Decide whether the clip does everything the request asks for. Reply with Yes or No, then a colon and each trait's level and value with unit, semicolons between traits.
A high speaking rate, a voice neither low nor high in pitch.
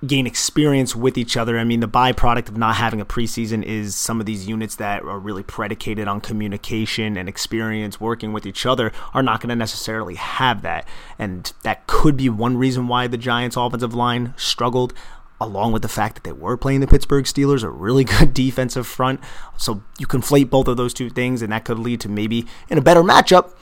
No: fast, 215 wpm; low, 120 Hz